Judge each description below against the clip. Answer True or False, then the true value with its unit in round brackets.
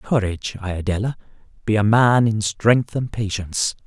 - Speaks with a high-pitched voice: False (105 Hz)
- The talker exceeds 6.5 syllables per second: False (5.0 syllables/s)